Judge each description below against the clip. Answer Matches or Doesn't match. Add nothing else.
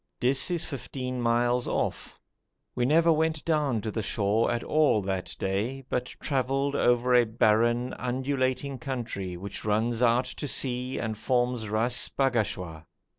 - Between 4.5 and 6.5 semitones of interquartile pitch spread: Doesn't match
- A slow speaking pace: Doesn't match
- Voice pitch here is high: Doesn't match